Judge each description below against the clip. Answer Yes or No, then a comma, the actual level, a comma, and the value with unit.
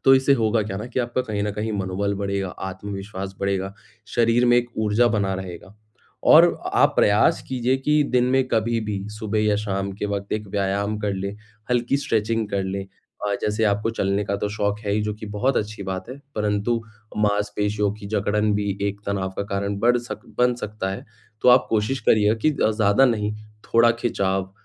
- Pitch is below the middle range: Yes, low, 105 Hz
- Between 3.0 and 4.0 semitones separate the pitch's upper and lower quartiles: No, narrow, 2.5 semitones